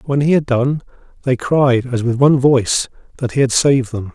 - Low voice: Yes, low, 130 Hz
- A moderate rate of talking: No, fast, 215 wpm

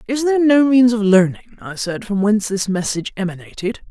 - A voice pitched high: Yes, high, 215 Hz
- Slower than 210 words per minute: Yes, average, 200 wpm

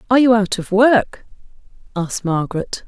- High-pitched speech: Yes, high, 210 Hz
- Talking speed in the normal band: Yes, average, 145 wpm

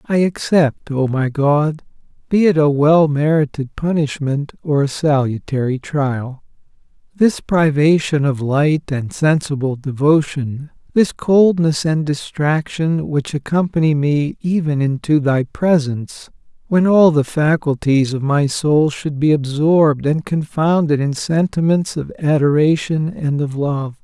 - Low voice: No, medium, 150 Hz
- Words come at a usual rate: No, slow, 125 wpm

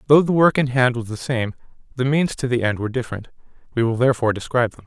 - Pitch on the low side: Yes, low, 125 Hz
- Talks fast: Yes, fast, 245 wpm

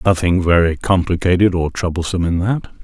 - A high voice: No, very low, 90 Hz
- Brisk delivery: No, average, 150 wpm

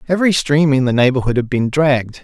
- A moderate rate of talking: No, fast, 215 wpm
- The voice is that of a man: Yes, male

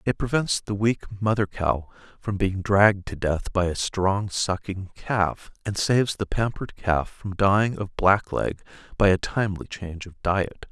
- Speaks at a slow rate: No, average, 175 wpm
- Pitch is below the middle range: Yes, low, 100 Hz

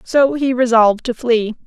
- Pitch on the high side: Yes, high, 245 Hz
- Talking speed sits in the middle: Yes, average, 180 wpm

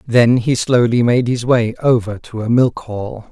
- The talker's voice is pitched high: No, low, 115 Hz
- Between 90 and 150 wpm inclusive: No, average, 200 wpm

